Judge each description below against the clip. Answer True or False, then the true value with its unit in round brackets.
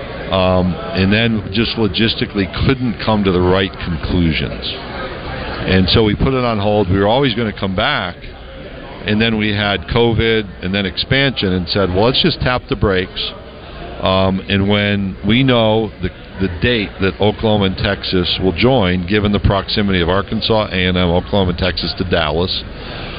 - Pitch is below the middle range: True (100 Hz)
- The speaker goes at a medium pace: True (170 wpm)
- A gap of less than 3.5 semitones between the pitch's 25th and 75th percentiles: True (3.0 semitones)